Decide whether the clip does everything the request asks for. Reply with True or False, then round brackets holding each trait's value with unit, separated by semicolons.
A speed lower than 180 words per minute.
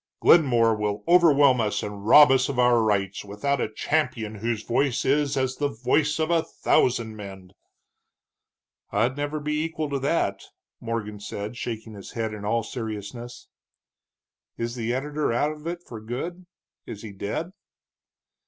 True (155 wpm)